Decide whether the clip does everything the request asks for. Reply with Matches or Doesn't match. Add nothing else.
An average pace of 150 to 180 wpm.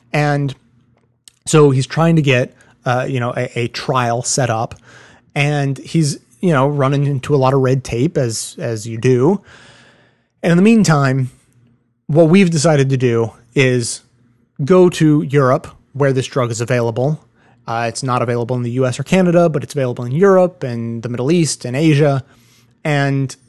Matches